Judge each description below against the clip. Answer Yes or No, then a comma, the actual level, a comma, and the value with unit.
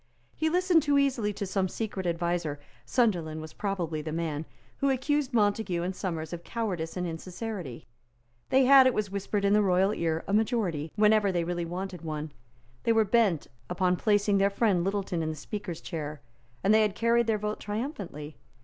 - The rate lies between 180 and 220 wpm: Yes, average, 185 wpm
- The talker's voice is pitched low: No, high, 195 Hz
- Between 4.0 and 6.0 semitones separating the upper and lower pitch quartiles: Yes, average, 4.5 semitones